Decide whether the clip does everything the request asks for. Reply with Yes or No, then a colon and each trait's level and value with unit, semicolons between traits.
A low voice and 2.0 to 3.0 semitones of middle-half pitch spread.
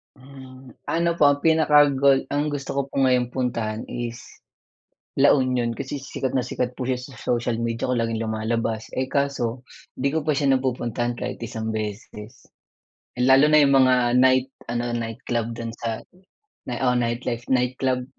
Yes: low, 125 Hz; narrow, 2.5 semitones